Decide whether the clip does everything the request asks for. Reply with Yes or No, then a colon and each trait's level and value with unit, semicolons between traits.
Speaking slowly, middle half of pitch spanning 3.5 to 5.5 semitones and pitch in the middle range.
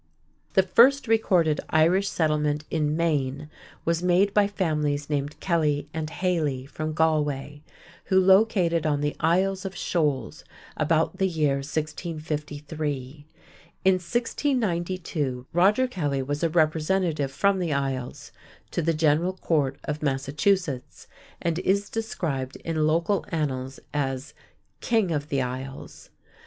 Yes: slow, 125 wpm; average, 3.9 semitones; medium, 155 Hz